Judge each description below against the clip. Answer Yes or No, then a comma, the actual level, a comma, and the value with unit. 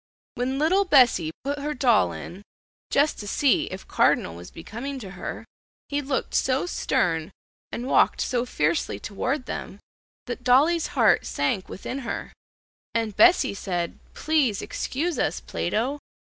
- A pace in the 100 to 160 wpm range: Yes, average, 145 wpm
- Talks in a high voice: Yes, very high, 250 Hz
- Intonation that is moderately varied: No, wide, 6.5 semitones